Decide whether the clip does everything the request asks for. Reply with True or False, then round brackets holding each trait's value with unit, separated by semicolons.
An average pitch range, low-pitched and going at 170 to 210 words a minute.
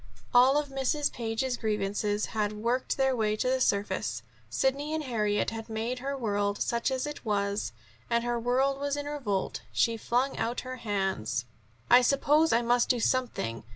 False (4.1 semitones; 235 Hz; 175 wpm)